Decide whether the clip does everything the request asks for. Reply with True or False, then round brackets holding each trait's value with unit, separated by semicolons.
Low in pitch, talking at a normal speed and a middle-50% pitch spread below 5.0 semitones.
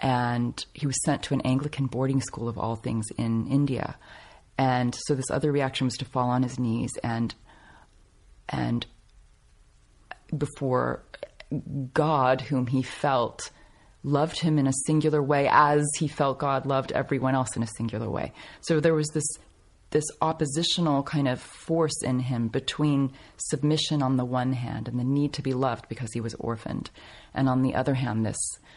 True (130 Hz; 170 wpm; 3.6 semitones)